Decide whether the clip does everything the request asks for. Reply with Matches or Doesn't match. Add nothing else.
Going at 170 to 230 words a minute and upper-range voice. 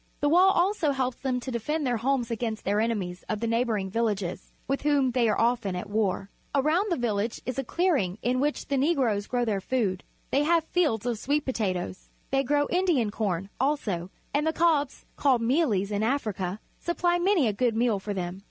Matches